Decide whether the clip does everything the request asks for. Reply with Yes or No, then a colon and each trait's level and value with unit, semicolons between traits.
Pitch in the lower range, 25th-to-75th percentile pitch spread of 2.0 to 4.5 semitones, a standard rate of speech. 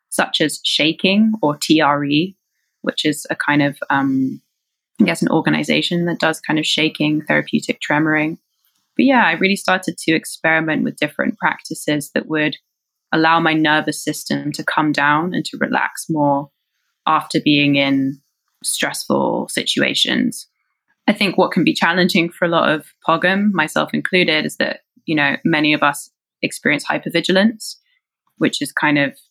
No: medium, 155 Hz; average, 2.9 semitones; average, 155 wpm